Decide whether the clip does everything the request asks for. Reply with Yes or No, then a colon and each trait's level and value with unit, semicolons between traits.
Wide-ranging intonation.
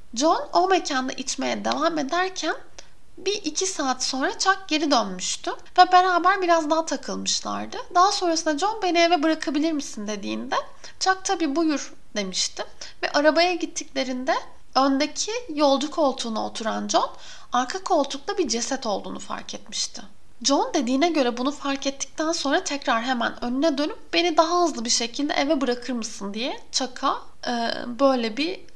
No: average, 4.9 semitones